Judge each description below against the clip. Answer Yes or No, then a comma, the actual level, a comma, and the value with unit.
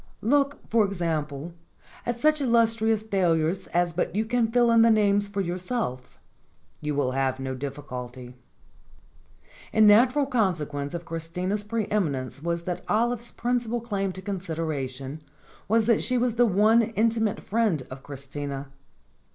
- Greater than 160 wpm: No, average, 145 wpm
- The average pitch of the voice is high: Yes, high, 195 Hz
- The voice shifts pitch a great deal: Yes, wide, 7.3 semitones